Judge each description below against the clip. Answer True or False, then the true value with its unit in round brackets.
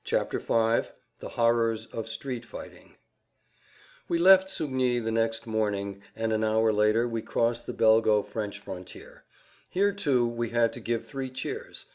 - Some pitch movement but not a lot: False (2.3 semitones)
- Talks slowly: False (160 wpm)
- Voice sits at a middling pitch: False (115 Hz)